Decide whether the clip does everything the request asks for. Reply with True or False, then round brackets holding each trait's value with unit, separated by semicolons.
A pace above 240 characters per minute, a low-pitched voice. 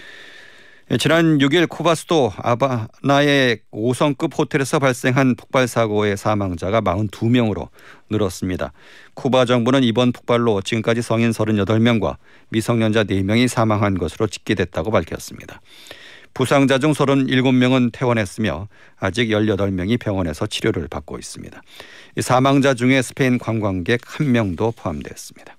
True (300 characters per minute; 120 Hz)